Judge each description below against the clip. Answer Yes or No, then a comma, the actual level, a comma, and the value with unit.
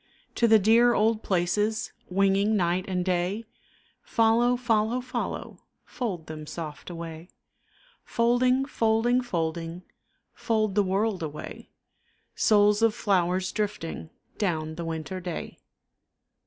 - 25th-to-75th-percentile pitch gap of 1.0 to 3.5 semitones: No, average, 4.4 semitones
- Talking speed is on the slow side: Yes, slow, 115 wpm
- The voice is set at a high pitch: Yes, high, 200 Hz